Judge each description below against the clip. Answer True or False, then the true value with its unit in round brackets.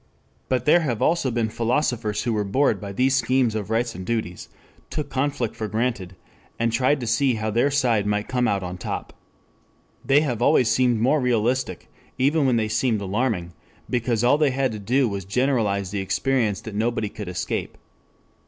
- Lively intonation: False (3.7 semitones)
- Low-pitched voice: True (115 Hz)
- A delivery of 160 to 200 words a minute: True (190 wpm)